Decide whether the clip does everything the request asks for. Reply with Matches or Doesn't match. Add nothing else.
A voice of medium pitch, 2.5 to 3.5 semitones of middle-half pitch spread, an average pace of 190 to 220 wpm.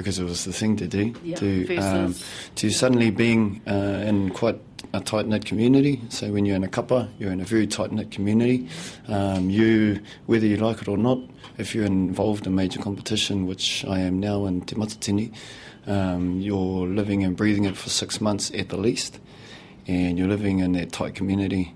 Doesn't match